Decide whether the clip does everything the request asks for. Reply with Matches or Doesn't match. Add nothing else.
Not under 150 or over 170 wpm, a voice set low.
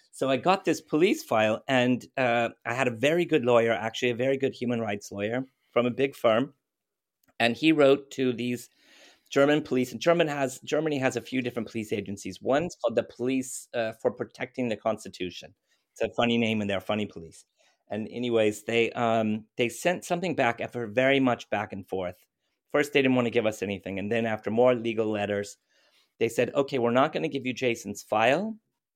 Doesn't match